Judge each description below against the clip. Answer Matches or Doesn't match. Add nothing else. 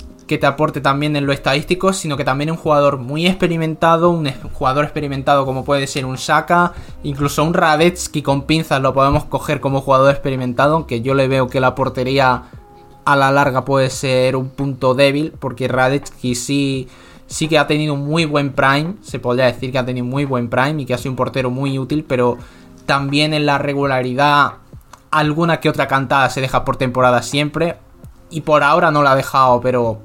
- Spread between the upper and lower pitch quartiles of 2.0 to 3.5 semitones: Matches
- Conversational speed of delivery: Doesn't match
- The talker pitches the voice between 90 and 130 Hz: Doesn't match